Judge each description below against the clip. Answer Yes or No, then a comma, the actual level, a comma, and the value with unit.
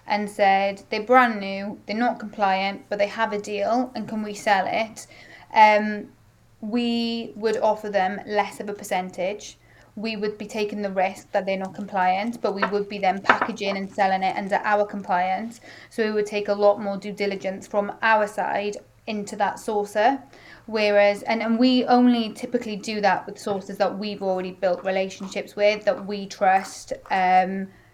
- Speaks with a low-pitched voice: No, high, 205 Hz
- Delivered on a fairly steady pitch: Yes, narrow, 1.9 semitones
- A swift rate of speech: No, average, 180 wpm